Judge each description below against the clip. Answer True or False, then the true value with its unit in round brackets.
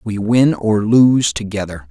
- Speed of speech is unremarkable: True (155 wpm)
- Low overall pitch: True (110 Hz)